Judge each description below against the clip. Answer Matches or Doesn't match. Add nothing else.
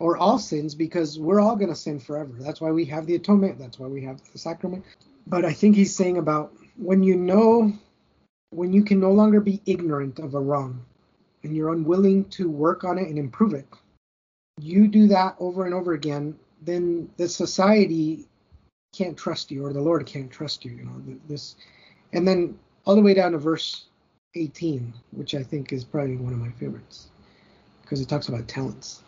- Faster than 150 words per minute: Matches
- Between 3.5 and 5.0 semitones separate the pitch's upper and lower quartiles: Matches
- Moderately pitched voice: Matches